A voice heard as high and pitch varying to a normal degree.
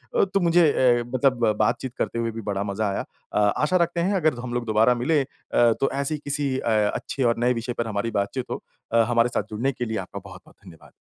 No: low, 120 Hz; average, 4.0 semitones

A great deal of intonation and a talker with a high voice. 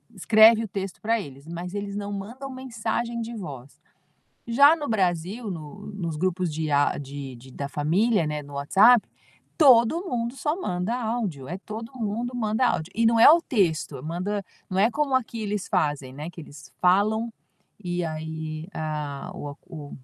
Yes: wide, 6.6 semitones; high, 195 Hz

